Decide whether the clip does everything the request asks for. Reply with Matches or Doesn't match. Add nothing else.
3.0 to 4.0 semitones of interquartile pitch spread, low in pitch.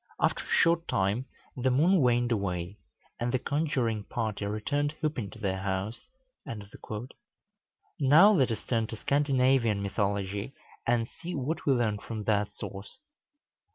Doesn't match